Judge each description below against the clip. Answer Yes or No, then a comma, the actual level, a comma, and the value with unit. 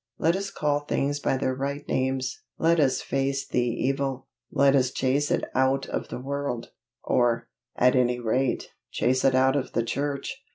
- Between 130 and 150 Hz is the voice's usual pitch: Yes, low, 135 Hz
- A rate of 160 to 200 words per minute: Yes, average, 175 wpm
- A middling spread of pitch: No, narrow, 1.8 semitones